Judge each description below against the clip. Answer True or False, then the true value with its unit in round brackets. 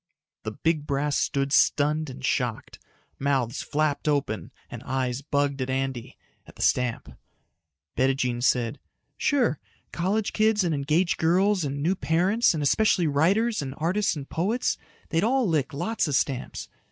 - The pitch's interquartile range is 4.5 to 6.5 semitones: True (5.1 semitones)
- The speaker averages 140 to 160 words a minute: True (150 wpm)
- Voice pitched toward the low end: False (145 Hz)